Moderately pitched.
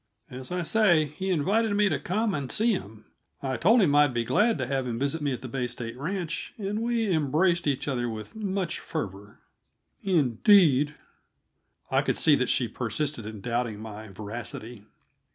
Yes: medium, 145 Hz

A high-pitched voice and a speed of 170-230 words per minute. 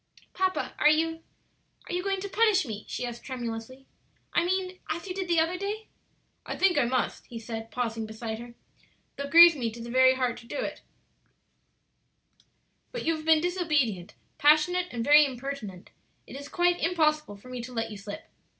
Yes: very high, 285 Hz; average, 190 wpm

